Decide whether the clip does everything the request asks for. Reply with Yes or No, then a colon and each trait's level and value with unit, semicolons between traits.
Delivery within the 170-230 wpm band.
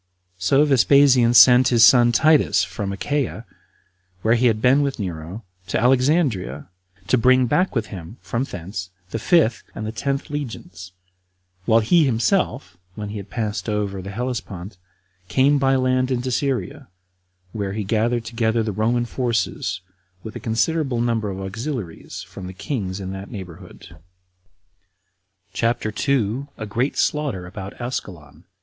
No: average, 145 wpm